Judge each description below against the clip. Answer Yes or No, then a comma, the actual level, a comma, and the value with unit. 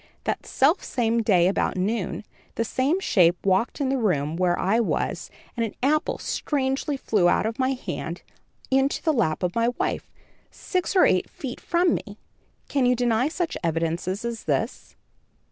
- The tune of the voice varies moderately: No, wide, 6.4 semitones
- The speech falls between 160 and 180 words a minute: Yes, average, 165 wpm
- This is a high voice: Yes, high, 230 Hz